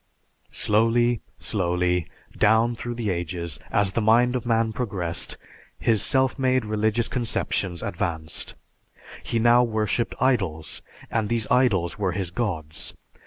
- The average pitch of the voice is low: Yes, low, 110 Hz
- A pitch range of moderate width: Yes, average, 4.9 semitones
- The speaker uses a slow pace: Yes, slow, 125 wpm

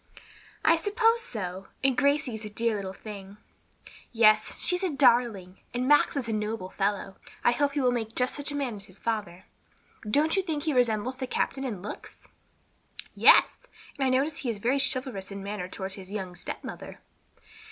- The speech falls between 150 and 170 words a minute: No, average, 190 wpm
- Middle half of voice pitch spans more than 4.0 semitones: Yes, wide, 5.5 semitones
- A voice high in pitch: Yes, high, 235 Hz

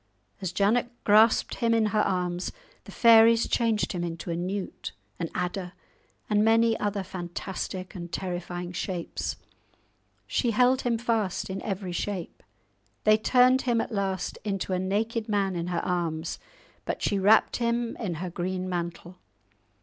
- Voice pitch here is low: No, high, 195 Hz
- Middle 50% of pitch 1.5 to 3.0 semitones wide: No, average, 4.0 semitones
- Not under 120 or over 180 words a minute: Yes, average, 150 wpm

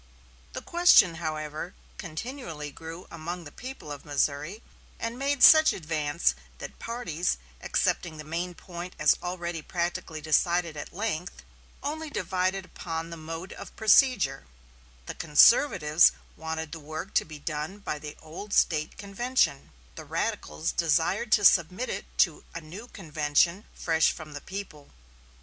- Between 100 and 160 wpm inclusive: Yes, average, 140 wpm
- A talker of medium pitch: Yes, medium, 170 Hz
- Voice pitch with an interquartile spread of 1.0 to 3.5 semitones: No, average, 4.3 semitones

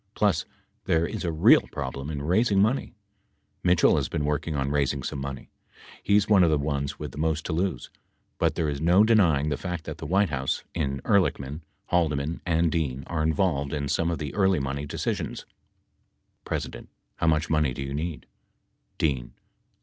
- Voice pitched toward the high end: No, very low, 80 Hz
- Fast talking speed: No, average, 160 wpm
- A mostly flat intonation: No, average, 3.9 semitones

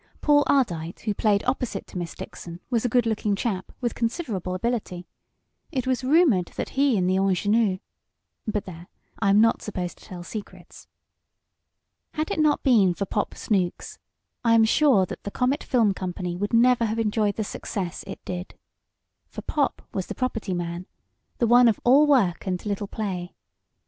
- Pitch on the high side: Yes, high, 210 Hz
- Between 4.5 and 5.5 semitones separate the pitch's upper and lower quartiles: Yes, average, 4.8 semitones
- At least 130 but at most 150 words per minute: No, average, 175 wpm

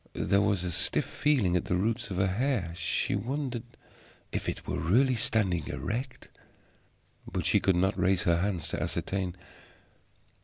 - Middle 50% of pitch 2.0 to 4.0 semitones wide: No, average, 4.6 semitones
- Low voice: Yes, very low, 95 Hz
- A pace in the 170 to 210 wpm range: No, average, 160 wpm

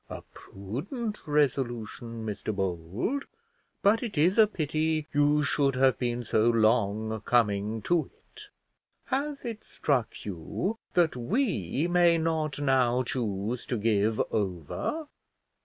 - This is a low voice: Yes, low, 130 Hz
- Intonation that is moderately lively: No, wide, 7.2 semitones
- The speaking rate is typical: No, slow, 125 wpm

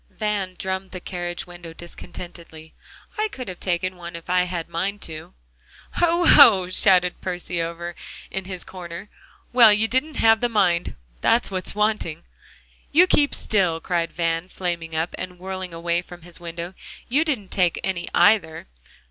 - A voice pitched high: No, medium, 180 Hz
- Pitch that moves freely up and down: No, average, 3.2 semitones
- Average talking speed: Yes, average, 170 wpm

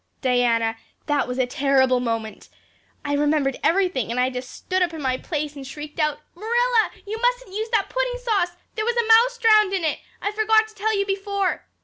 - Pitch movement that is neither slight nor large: No, wide, 8.4 semitones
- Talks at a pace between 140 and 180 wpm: No, fast, 205 wpm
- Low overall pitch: No, very high, 365 Hz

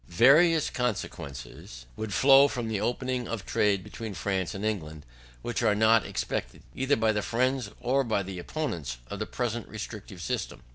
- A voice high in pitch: No, low, 110 Hz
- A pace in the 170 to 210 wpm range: No, average, 160 wpm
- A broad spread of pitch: No, average, 4.8 semitones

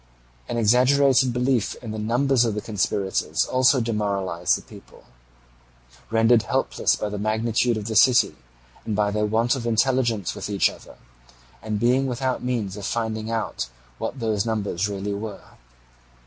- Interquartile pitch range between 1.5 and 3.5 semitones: Yes, average, 2.8 semitones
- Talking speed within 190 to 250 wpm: No, average, 155 wpm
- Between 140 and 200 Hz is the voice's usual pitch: No, low, 110 Hz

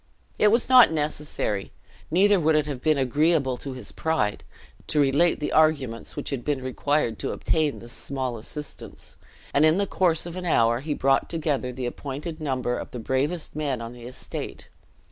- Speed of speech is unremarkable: Yes, average, 185 wpm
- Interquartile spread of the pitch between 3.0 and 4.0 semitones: Yes, average, 3.7 semitones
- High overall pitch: No, medium, 145 Hz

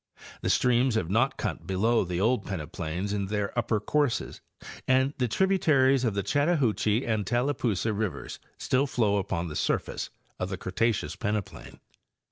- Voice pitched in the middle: No, low, 110 Hz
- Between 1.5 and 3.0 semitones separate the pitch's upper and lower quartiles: No, average, 4.6 semitones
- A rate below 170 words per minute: Yes, average, 150 wpm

